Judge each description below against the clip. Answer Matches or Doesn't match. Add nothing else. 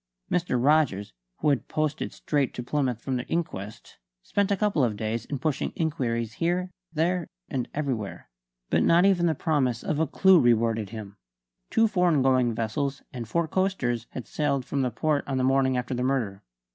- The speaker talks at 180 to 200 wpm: Matches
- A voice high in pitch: Doesn't match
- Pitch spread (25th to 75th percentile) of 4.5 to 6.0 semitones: Matches